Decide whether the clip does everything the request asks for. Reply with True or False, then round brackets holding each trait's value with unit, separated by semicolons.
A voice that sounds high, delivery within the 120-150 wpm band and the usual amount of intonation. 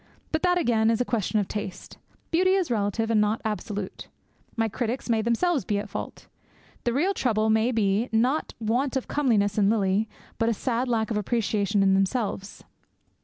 False (225 Hz; 185 wpm; 3.1 semitones)